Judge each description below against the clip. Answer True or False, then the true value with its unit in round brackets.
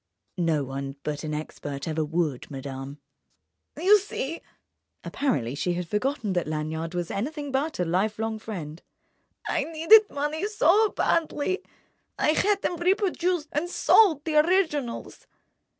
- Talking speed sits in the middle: False (125 wpm)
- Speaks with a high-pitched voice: True (260 Hz)